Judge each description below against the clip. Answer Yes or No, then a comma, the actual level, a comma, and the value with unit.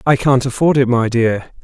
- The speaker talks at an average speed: No, fast, 220 wpm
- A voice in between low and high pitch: No, low, 125 Hz